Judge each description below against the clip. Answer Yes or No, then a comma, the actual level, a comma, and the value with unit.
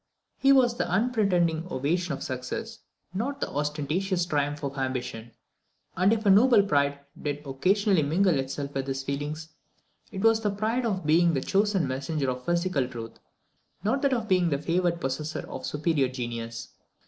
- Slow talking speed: No, average, 165 wpm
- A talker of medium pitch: Yes, medium, 165 Hz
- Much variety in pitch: Yes, wide, 6.2 semitones